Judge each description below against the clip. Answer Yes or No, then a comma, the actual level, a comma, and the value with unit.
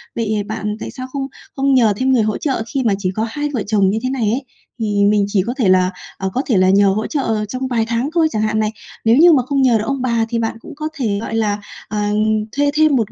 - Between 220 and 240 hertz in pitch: Yes, high, 225 Hz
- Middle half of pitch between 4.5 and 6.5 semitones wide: No, average, 3.9 semitones